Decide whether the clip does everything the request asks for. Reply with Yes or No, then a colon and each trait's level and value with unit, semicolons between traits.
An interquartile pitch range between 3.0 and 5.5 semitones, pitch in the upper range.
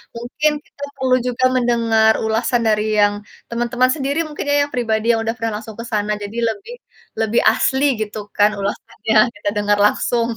No: narrow, 2.6 semitones; high, 230 Hz